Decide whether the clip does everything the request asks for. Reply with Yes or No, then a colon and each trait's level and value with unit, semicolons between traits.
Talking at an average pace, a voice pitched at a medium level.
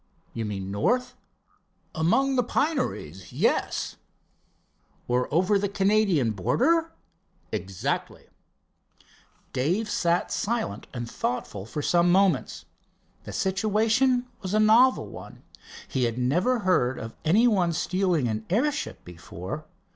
No: slow, 115 wpm; medium, 180 Hz